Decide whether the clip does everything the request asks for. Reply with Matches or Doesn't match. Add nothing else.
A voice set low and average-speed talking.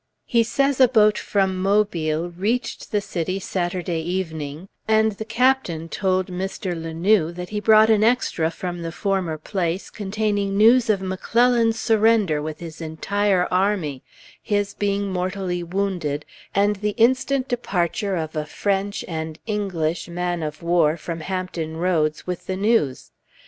Doesn't match